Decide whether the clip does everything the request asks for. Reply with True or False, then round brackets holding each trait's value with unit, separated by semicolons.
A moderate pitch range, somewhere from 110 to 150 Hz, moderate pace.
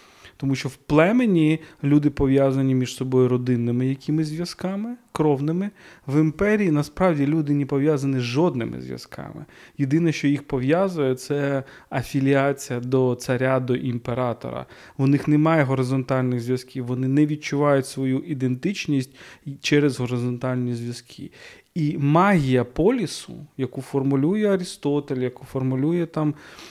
True (3.2 semitones; 140 Hz; 120 wpm)